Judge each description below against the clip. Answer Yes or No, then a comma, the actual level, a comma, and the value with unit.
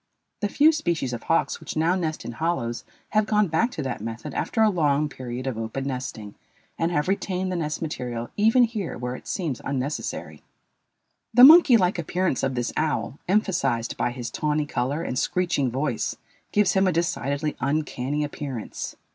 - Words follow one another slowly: No, average, 175 wpm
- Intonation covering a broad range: Yes, wide, 6.3 semitones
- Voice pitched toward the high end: No, medium, 150 Hz